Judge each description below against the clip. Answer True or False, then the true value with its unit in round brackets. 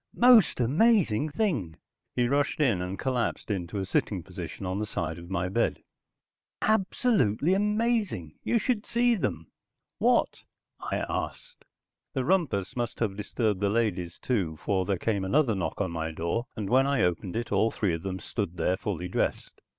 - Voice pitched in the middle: False (105 Hz)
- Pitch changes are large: True (7.8 semitones)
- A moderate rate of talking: True (170 wpm)